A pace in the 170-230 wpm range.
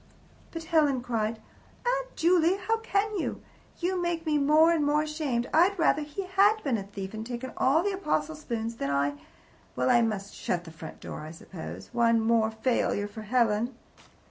Yes: average, 190 wpm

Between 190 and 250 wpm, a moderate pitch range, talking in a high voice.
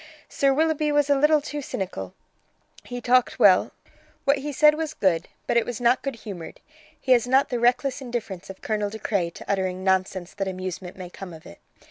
No: average, 200 wpm; wide, 6.5 semitones; high, 235 Hz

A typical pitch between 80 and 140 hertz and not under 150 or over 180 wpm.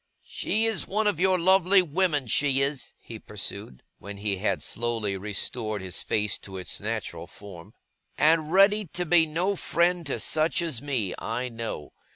Yes: low, 135 Hz; average, 170 wpm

